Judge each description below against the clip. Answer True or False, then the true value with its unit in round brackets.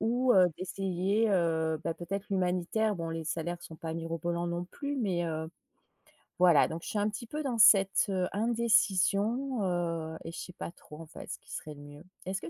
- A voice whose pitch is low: False (180 Hz)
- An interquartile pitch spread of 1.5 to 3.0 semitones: False (4.0 semitones)